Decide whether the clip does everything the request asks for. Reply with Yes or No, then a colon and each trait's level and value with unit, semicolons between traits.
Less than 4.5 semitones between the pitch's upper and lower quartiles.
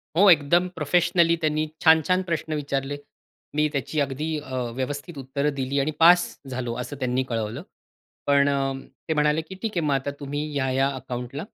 Yes: average, 3.0 semitones